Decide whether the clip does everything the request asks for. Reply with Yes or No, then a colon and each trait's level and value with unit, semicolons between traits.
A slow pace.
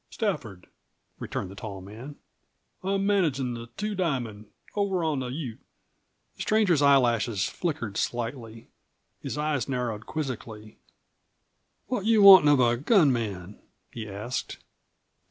Yes: slow, 125 wpm